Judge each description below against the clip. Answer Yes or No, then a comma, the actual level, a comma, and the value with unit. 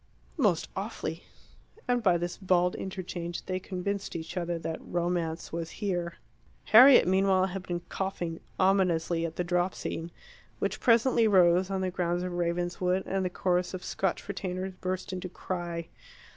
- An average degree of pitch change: No, narrow, 1.7 semitones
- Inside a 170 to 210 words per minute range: No, average, 155 wpm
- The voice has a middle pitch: Yes, medium, 180 Hz